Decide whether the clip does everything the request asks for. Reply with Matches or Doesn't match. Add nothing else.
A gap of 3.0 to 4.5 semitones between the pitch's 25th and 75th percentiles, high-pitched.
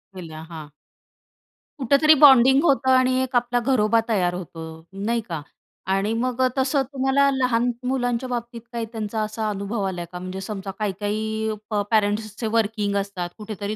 Matches